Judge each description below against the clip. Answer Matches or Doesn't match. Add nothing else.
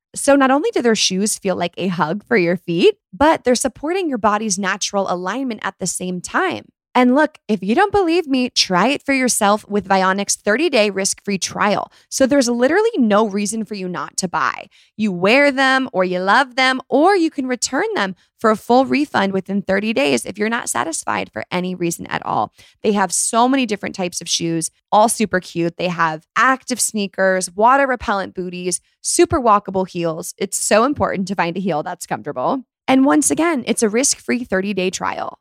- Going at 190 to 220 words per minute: Matches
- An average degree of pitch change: Doesn't match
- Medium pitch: Doesn't match